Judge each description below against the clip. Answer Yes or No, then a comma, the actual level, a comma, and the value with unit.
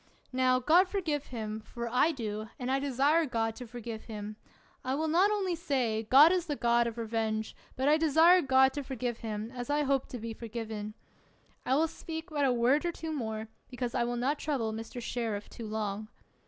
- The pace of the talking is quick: Yes, fast, 210 wpm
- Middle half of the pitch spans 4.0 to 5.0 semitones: Yes, average, 4.7 semitones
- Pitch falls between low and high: No, very high, 250 Hz